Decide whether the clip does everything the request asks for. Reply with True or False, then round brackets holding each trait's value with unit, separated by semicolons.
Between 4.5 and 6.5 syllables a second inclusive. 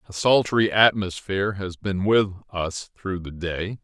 False (4.2 syllables/s)